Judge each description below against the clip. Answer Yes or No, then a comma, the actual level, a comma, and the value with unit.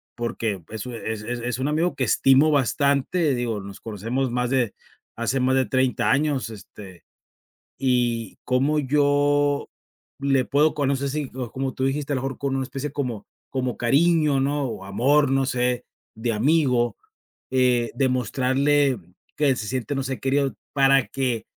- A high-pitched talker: No, low, 130 Hz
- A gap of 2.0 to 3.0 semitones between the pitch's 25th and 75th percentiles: Yes, narrow, 2.6 semitones